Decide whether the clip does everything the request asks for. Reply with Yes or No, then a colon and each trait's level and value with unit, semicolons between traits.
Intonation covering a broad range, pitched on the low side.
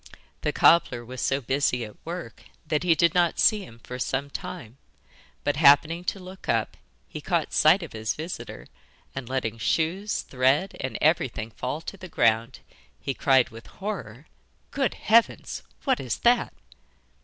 No: wide, 6.1 semitones; medium, 145 Hz